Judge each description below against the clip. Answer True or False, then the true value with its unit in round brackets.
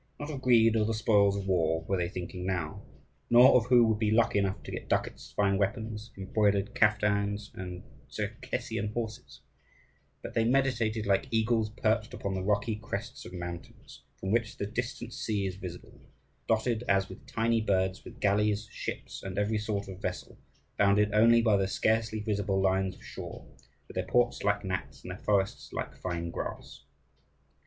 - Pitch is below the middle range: True (105 Hz)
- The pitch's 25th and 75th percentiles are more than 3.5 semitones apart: False (2.6 semitones)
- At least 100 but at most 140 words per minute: False (175 wpm)